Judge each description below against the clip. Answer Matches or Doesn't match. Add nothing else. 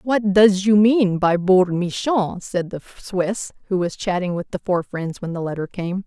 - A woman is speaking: Matches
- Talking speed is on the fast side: Matches